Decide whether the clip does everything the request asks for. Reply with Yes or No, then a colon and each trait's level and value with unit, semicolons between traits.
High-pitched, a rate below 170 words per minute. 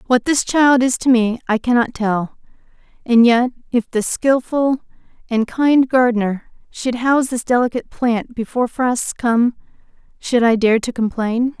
Yes: high, 240 Hz; average, 155 wpm